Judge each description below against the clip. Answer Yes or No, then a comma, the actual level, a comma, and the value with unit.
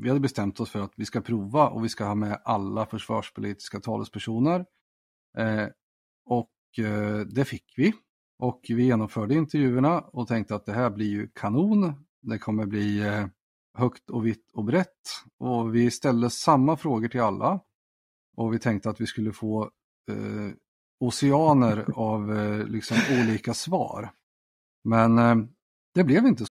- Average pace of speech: Yes, average, 160 wpm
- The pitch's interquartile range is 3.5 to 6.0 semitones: No, average, 2.9 semitones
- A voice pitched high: No, low, 115 Hz